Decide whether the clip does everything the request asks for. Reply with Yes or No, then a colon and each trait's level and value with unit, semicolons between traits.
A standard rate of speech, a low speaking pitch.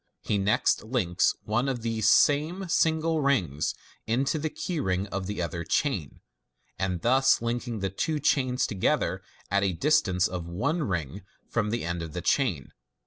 Yes: average, 160 wpm; low, 110 Hz